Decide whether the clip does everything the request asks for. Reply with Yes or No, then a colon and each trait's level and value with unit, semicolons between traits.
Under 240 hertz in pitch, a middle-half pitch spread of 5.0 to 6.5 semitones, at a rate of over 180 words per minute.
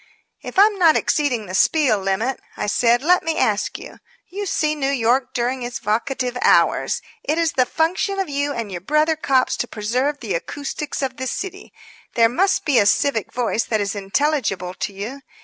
No: very high, 260 Hz; wide, 5.5 semitones; average, 190 wpm